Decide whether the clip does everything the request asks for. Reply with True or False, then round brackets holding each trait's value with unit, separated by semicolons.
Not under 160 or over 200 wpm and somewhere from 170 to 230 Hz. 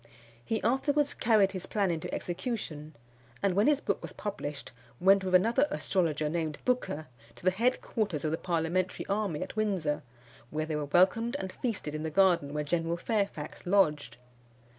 True (165 wpm; 185 Hz)